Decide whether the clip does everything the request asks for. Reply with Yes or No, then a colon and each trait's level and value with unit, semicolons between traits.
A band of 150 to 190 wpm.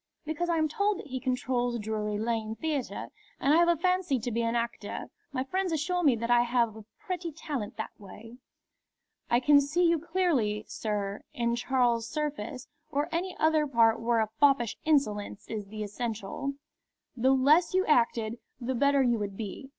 Yes: average, 180 wpm